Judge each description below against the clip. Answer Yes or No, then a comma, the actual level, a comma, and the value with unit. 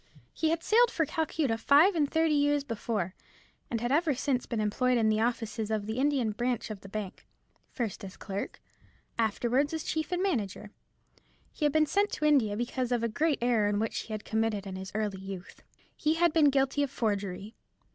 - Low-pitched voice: No, high, 240 Hz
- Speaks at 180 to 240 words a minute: Yes, average, 195 wpm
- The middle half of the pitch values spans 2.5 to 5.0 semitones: No, wide, 5.6 semitones